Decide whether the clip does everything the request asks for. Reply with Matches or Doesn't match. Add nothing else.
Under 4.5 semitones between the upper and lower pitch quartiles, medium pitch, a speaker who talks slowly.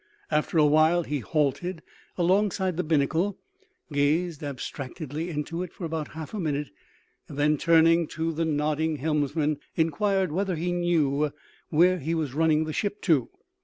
Doesn't match